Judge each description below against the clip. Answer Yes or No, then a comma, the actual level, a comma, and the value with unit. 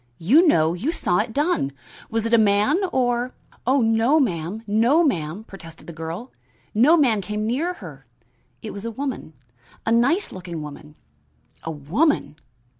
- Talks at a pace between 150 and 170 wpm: Yes, average, 165 wpm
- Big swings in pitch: Yes, wide, 7.7 semitones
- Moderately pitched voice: No, high, 220 Hz